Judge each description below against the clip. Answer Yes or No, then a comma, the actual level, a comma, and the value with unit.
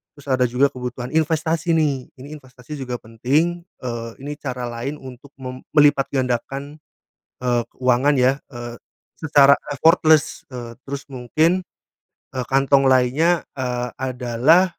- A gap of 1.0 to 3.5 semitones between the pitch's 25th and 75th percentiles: Yes, average, 3.0 semitones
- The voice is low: Yes, low, 130 Hz